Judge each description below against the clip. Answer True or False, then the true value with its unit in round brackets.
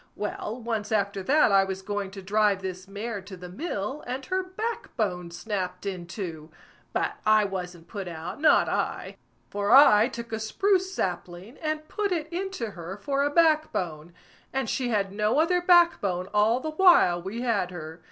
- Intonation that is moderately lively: False (7.0 semitones)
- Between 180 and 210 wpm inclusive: True (185 wpm)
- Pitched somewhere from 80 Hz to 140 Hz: False (210 Hz)